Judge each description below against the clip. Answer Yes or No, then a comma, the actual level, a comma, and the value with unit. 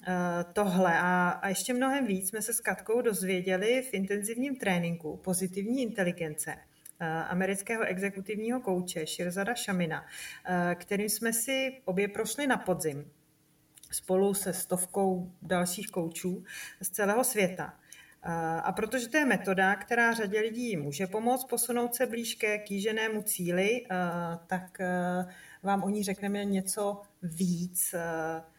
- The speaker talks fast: No, average, 120 wpm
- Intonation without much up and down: No, average, 3.4 semitones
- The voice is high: Yes, high, 195 Hz